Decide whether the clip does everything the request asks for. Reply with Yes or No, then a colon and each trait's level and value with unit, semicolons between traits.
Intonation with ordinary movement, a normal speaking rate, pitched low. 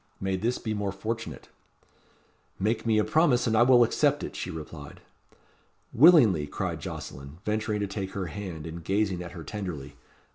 Yes: average, 4.8 semitones; average, 170 wpm; low, 100 Hz